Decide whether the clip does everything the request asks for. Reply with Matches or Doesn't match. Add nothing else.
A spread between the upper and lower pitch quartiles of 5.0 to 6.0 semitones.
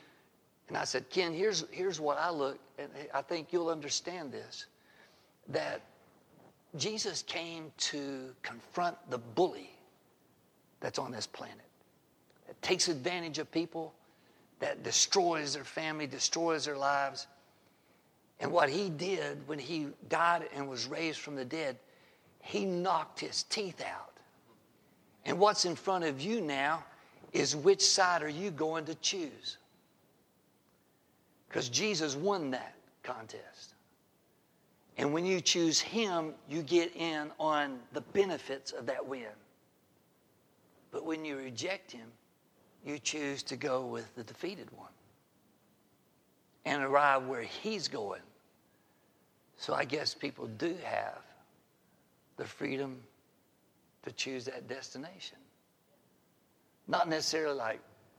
Doesn't match